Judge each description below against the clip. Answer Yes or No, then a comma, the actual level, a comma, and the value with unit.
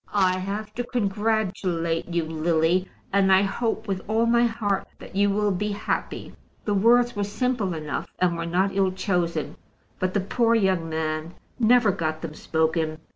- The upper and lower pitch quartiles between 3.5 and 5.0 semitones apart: Yes, average, 4.1 semitones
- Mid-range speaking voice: No, high, 195 Hz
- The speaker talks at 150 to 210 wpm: Yes, average, 170 wpm